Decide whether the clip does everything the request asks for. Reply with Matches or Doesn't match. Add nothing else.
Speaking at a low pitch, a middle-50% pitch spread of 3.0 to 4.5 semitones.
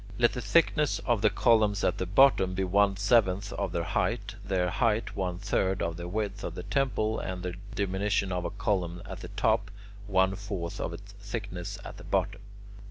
Doesn't match